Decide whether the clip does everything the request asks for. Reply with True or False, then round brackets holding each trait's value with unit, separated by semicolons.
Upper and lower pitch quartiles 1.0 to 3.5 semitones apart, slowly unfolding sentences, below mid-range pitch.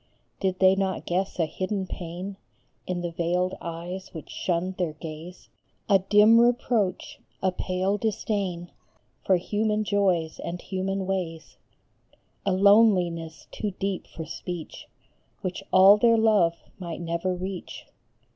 False (2.4 semitones; 130 wpm; 185 Hz)